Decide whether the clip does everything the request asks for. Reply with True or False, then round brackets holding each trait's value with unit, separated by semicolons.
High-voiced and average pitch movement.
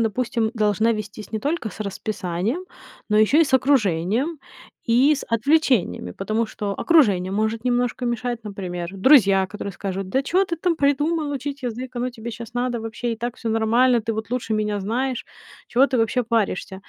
True (230 Hz; 3.6 semitones)